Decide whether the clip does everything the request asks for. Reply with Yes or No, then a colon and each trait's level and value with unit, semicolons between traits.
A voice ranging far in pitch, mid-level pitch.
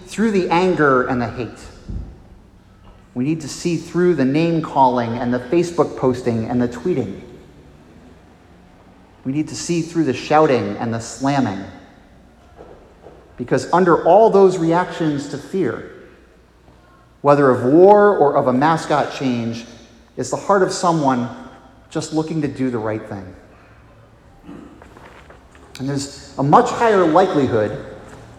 No: wide, 7.3 semitones; low, 130 Hz